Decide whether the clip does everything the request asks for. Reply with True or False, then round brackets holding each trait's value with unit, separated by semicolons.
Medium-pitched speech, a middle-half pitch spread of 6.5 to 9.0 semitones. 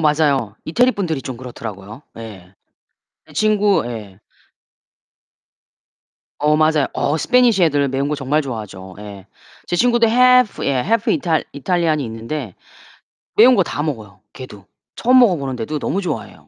True (145 Hz; 8.6 semitones)